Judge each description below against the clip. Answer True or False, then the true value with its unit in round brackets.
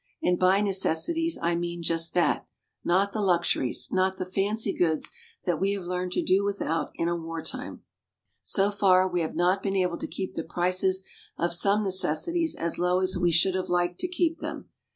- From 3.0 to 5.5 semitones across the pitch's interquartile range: False (2.4 semitones)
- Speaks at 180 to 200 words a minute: True (190 wpm)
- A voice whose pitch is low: False (185 Hz)